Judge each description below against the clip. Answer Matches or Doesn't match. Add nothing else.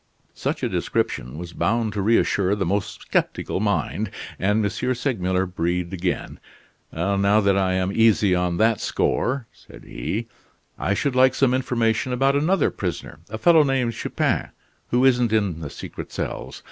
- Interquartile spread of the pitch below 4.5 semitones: Doesn't match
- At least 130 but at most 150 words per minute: Doesn't match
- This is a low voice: Matches